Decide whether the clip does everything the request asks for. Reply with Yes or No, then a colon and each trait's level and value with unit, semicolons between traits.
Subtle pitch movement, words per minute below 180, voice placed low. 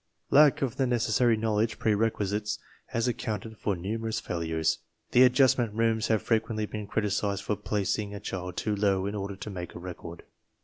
Yes: narrow, 2.2 semitones; average, 170 wpm; low, 105 Hz